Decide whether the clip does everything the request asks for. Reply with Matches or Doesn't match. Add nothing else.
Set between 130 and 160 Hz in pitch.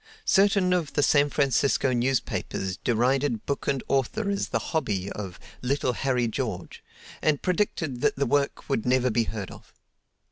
Matches